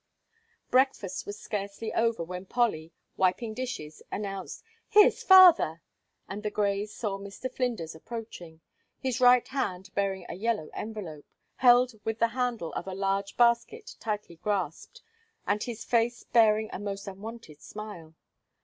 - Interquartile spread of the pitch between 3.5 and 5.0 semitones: Yes, average, 3.8 semitones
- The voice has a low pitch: No, high, 210 Hz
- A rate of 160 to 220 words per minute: No, average, 140 wpm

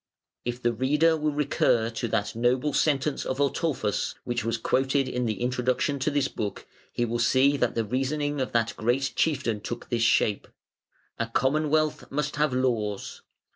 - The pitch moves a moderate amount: Yes, average, 3.5 semitones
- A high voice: No, low, 130 Hz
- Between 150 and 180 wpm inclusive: Yes, average, 170 wpm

